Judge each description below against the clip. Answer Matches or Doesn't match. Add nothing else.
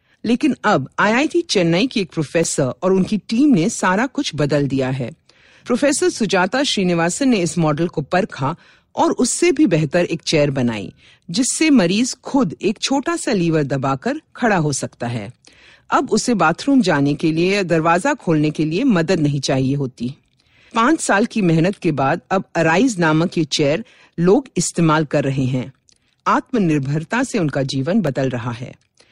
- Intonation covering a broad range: Matches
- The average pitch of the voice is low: Doesn't match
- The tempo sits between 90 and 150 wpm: Doesn't match